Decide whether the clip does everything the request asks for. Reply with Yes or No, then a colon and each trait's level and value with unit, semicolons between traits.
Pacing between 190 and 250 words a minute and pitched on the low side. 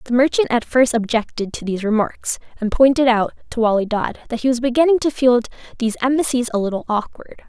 No: average, 200 wpm; high, 240 Hz